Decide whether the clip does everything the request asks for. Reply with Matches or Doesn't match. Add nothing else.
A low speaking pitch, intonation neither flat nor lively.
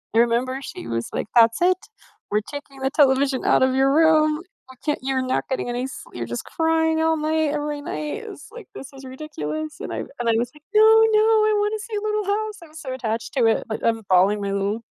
Doesn't match